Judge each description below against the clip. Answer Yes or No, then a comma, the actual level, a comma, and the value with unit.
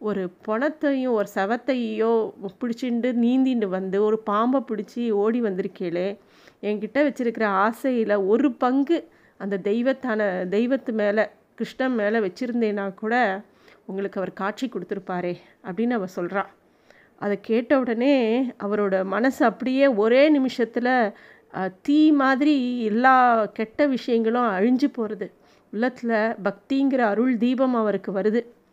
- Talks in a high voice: Yes, high, 225 Hz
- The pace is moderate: Yes, average, 110 wpm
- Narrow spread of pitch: No, average, 3.8 semitones